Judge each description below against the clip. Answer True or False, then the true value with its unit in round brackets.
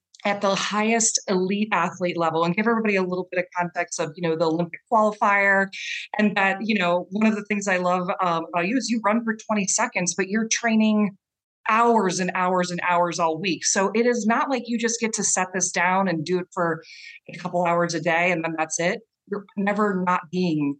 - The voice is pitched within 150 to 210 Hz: True (190 Hz)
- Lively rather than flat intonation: False (3.4 semitones)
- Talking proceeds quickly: True (225 wpm)